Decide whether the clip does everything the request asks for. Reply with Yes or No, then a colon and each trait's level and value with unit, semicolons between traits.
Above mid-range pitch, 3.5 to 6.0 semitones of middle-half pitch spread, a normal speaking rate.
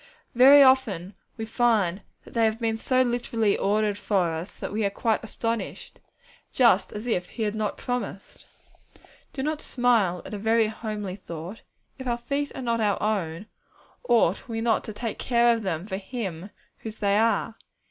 No: high, 220 Hz; average, 3.0 semitones; average, 180 wpm